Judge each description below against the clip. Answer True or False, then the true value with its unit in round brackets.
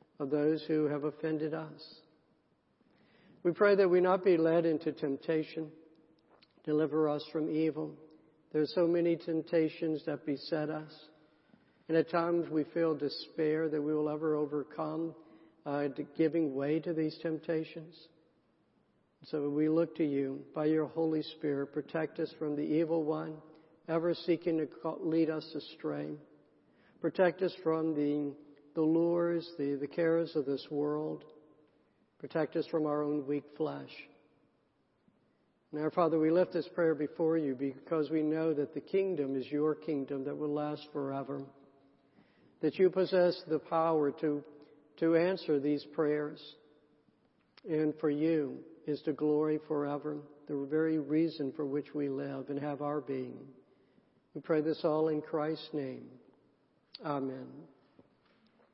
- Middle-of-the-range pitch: True (155 Hz)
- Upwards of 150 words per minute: False (145 wpm)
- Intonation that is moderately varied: False (1.5 semitones)